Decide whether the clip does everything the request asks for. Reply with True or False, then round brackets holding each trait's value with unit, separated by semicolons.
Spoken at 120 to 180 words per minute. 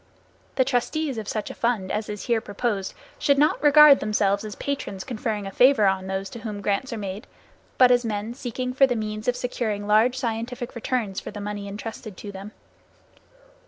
False (195 wpm)